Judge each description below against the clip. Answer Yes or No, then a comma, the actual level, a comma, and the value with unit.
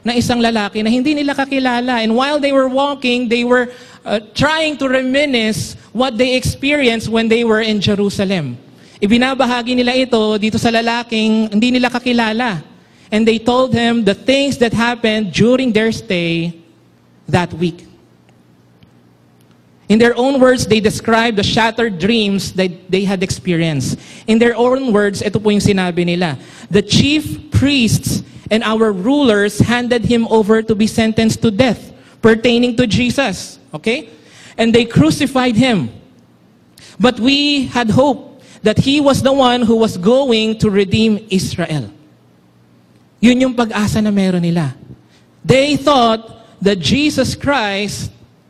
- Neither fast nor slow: Yes, average, 145 wpm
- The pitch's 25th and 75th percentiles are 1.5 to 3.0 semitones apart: No, average, 3.8 semitones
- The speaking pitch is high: Yes, high, 225 Hz